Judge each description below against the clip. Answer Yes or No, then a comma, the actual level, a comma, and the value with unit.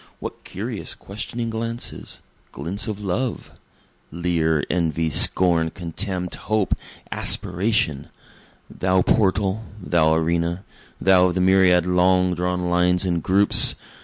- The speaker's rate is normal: No, slow, 110 wpm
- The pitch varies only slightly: Yes, narrow, 2.3 semitones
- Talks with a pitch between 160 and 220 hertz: No, very low, 90 Hz